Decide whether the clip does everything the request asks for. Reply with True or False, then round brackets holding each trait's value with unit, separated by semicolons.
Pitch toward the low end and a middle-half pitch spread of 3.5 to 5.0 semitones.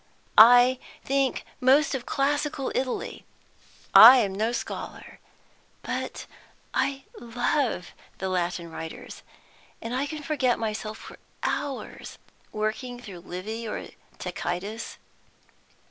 False (240 Hz; 4.5 semitones)